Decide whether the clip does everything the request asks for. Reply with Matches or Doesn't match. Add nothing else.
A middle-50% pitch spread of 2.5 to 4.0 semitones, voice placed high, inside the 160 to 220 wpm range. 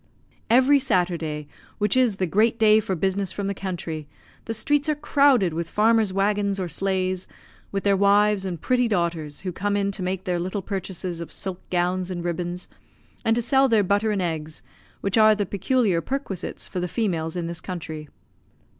Matches